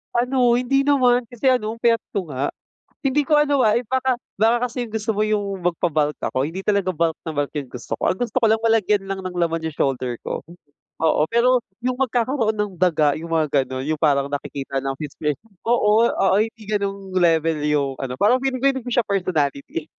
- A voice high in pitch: Yes, high, 200 Hz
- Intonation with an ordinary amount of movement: No, wide, 7.5 semitones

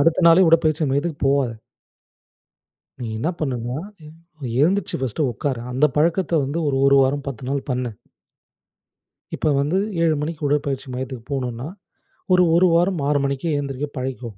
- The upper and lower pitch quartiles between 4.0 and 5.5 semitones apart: No, average, 3.6 semitones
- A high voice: No, medium, 140 Hz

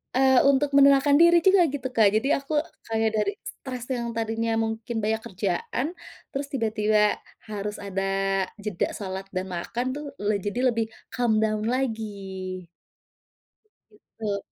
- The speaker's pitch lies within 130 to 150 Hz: No, high, 225 Hz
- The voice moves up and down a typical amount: Yes, average, 4.0 semitones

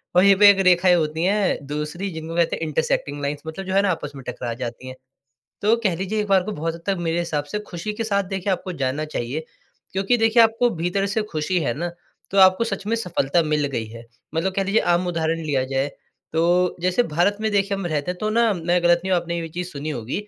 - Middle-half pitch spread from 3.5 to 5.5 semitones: Yes, average, 4.4 semitones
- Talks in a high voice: No, medium, 175 Hz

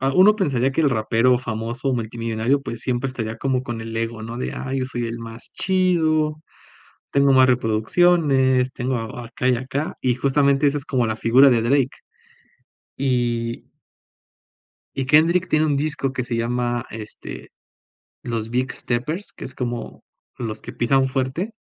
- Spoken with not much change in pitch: No, average, 3.0 semitones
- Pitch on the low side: Yes, low, 130 Hz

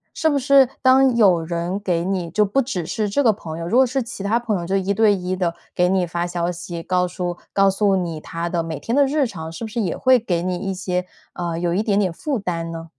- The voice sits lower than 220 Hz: Yes, medium, 185 Hz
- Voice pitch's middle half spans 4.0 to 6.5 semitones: Yes, average, 4.4 semitones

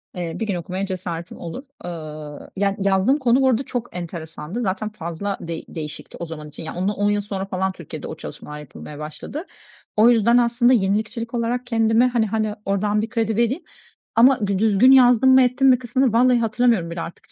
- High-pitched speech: Yes, high, 210 Hz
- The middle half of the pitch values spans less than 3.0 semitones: No, average, 5.3 semitones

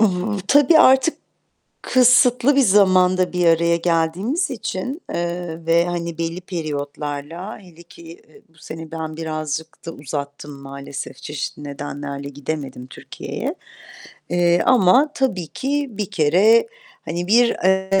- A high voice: No, medium, 170 Hz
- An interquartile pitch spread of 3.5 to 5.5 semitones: Yes, average, 4.6 semitones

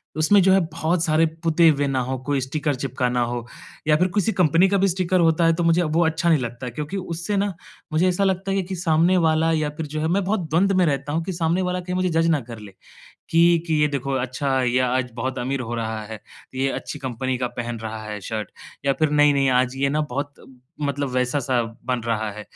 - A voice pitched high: No, medium, 150 Hz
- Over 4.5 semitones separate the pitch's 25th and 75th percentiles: Yes, average, 4.9 semitones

